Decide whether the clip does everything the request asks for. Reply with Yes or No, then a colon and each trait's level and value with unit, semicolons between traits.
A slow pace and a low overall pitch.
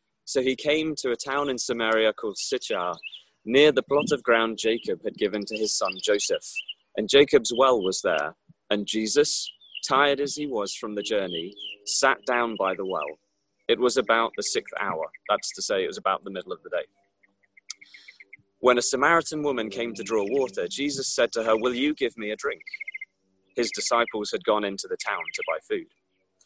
No: average, 195 wpm; low, 130 Hz